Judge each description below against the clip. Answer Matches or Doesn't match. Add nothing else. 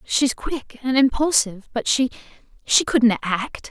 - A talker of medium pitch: Doesn't match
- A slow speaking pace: Matches